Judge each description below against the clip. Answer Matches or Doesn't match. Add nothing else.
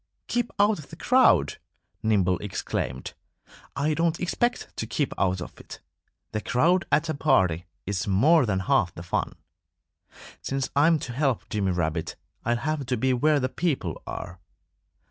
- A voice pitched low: Matches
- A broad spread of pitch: Matches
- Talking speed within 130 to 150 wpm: Doesn't match